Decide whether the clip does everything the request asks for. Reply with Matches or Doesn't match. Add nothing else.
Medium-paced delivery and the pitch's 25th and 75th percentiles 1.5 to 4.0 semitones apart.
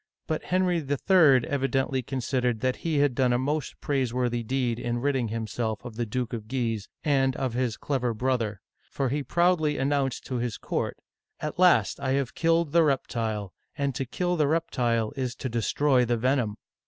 Matches